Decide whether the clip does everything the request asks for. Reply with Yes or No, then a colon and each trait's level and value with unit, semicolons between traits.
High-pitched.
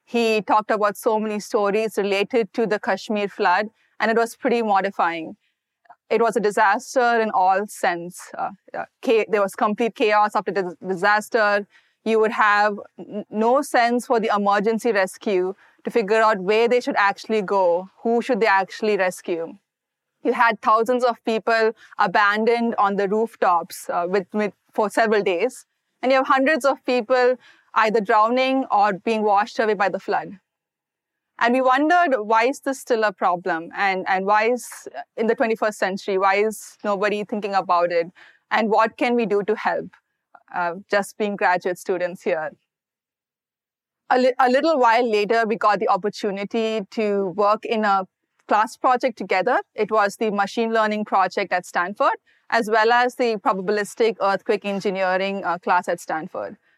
Yes: high, 215 Hz